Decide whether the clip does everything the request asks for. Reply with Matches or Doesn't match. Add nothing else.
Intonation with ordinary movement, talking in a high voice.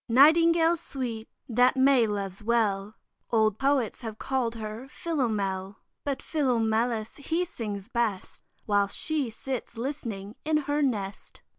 Matches